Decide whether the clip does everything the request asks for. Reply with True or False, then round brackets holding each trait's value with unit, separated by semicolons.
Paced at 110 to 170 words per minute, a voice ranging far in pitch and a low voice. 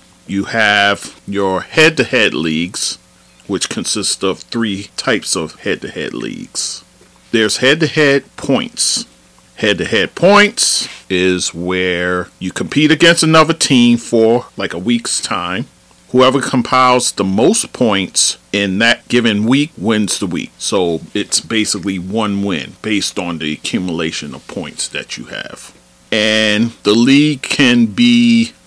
True (145 wpm; 6.3 semitones; 105 Hz)